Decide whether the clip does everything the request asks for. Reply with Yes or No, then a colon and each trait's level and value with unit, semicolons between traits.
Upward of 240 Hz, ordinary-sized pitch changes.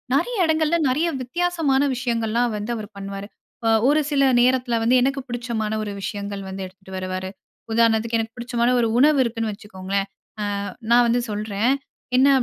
No: high, 235 Hz; average, 3.8 semitones